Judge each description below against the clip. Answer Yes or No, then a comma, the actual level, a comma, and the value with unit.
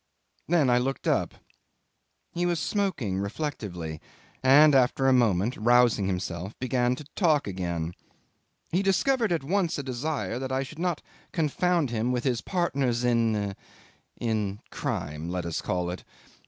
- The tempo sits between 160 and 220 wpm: No, average, 145 wpm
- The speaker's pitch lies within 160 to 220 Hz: No, low, 125 Hz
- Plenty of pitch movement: Yes, wide, 7.4 semitones